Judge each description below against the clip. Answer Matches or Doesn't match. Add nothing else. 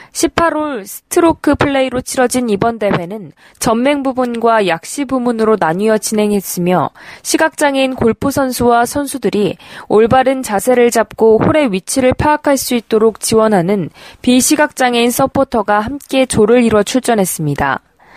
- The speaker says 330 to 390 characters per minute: Doesn't match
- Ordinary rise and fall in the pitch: Matches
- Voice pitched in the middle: Doesn't match